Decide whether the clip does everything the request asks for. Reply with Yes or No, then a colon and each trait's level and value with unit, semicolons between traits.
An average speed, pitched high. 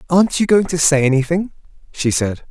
No: average, 190 wpm; medium, 160 Hz